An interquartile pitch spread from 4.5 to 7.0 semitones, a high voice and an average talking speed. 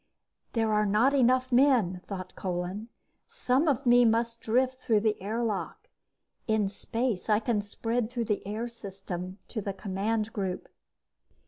No: average, 3.2 semitones; high, 220 Hz; average, 145 wpm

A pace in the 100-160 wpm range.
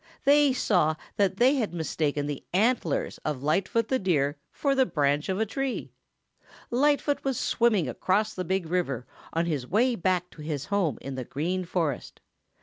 No: average, 170 wpm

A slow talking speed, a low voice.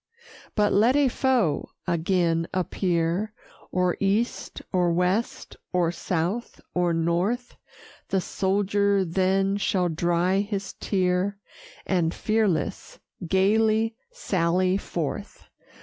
No: slow, 100 wpm; high, 190 Hz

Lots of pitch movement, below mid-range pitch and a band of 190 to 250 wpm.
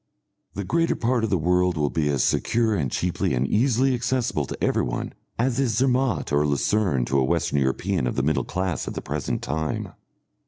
Yes: wide, 8.6 semitones; very low, 90 Hz; average, 195 wpm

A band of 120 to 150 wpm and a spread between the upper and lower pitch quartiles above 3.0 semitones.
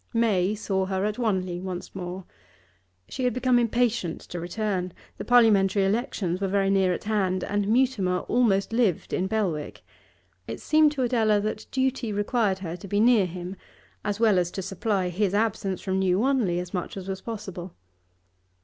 No: average, 175 wpm; average, 3.4 semitones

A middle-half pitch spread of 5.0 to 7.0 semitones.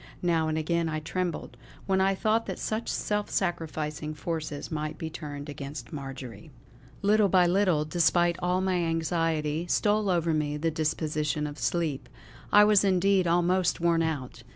No: average, 3.2 semitones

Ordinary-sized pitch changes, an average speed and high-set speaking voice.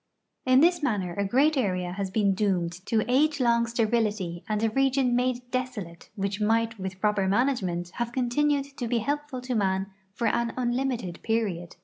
Yes: average, 4.7 semitones; average, 170 wpm; high, 230 Hz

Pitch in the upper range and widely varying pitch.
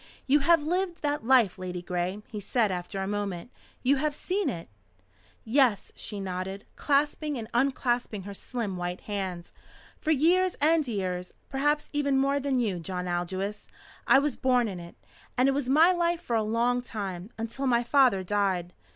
Yes: high, 235 Hz; wide, 6.6 semitones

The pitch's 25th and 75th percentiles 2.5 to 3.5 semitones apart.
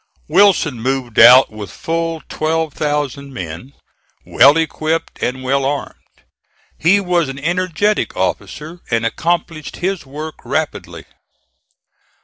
No: average, 4.0 semitones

